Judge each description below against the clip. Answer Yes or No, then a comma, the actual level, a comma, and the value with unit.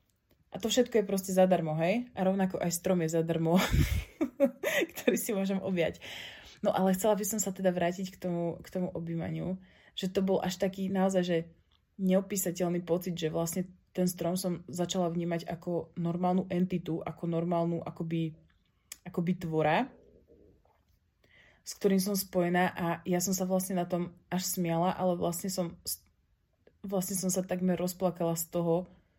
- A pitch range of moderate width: No, narrow, 1.9 semitones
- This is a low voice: No, medium, 180 Hz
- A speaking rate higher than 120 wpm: Yes, average, 160 wpm